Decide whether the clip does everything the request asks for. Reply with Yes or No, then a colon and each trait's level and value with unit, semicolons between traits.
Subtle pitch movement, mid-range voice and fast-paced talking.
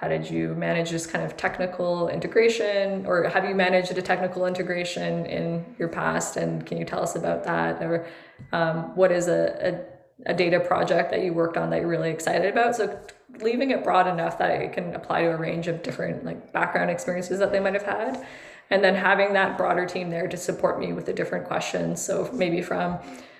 Yes: narrow, 2.3 semitones; medium, 180 Hz; fast, 215 wpm